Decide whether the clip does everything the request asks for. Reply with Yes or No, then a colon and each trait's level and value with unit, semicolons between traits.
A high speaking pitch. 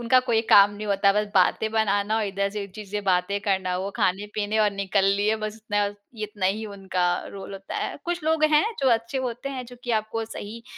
Yes: high, 210 Hz